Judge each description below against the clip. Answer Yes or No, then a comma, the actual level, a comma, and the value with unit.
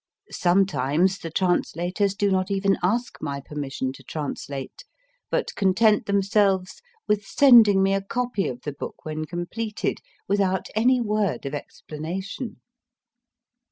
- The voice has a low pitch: No, high, 190 Hz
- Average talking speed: No, slow, 125 wpm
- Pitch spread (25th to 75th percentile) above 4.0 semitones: Yes, average, 4.4 semitones